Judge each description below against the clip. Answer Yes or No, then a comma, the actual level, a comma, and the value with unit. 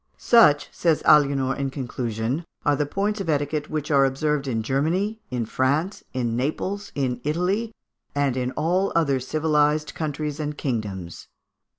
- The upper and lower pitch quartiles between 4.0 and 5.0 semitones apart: No, average, 3.3 semitones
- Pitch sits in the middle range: Yes, medium, 145 Hz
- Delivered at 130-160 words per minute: Yes, average, 150 wpm